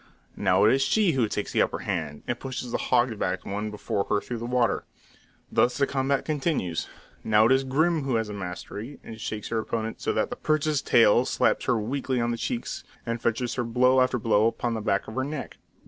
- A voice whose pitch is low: Yes, low, 120 Hz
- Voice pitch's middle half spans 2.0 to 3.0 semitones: No, average, 3.6 semitones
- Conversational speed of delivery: No, fast, 225 wpm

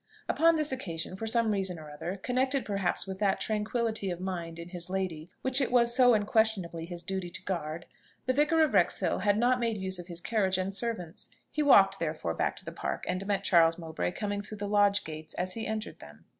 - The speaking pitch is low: No, high, 195 Hz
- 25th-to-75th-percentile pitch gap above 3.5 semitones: Yes, average, 4.4 semitones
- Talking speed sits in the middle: No, fast, 220 wpm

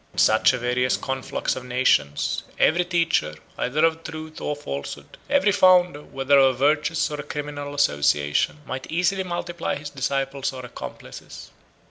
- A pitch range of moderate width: Yes, average, 4.2 semitones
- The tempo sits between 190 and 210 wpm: No, average, 155 wpm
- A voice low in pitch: No, medium, 145 Hz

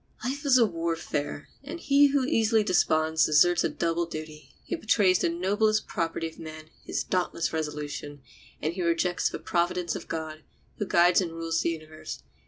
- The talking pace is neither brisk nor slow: Yes, average, 170 wpm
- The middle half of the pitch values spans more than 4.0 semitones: Yes, average, 4.6 semitones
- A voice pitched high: No, medium, 170 Hz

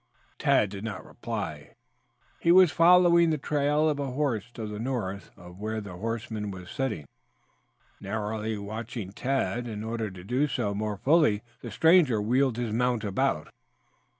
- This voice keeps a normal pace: Yes, average, 155 wpm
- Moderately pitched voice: No, low, 115 Hz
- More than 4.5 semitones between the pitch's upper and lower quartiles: Yes, average, 4.9 semitones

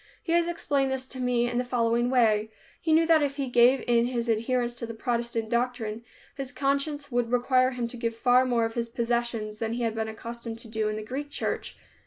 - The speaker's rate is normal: No, fast, 230 wpm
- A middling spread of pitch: No, narrow, 2.0 semitones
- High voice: Yes, high, 240 Hz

